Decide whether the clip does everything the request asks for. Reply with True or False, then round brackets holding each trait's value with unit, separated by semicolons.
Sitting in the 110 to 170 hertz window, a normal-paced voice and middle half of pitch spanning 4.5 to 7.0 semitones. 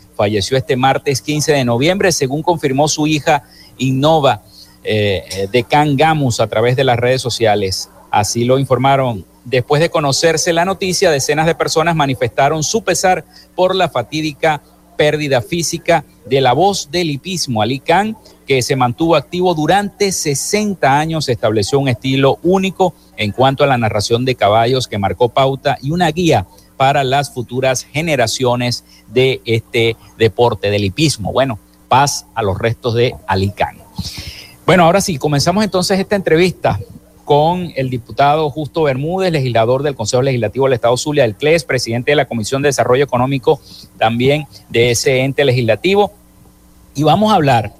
True (135 Hz; 155 wpm; 5.1 semitones)